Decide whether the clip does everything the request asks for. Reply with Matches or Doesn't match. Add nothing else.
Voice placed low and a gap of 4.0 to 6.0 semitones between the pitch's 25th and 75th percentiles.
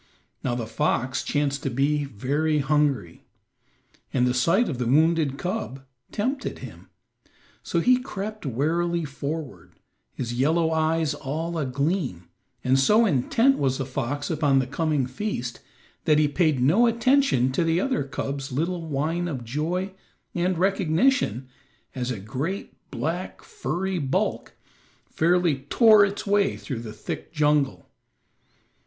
Doesn't match